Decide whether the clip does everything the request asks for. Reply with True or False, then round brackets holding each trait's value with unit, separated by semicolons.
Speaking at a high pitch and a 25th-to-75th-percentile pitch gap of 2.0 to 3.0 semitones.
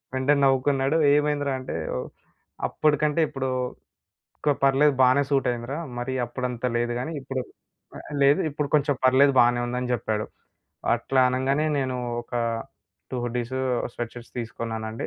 False (130 Hz; 2.6 semitones)